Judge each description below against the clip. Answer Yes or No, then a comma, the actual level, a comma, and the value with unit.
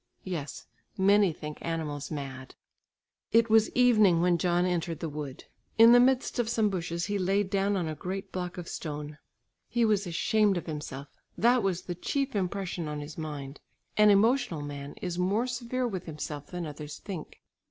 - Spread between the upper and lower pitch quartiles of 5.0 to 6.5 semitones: Yes, wide, 5.4 semitones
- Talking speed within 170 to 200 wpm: Yes, average, 175 wpm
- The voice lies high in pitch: No, medium, 180 Hz